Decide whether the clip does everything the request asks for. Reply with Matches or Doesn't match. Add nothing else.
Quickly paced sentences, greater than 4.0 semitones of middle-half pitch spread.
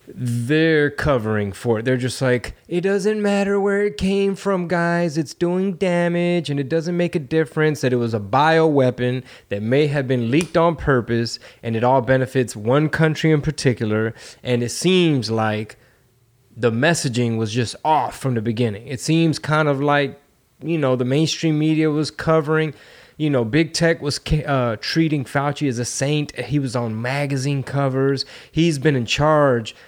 Doesn't match